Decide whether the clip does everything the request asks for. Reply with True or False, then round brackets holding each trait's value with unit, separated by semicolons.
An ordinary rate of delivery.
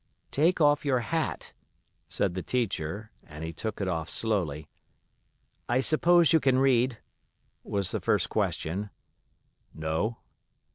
False (130 wpm)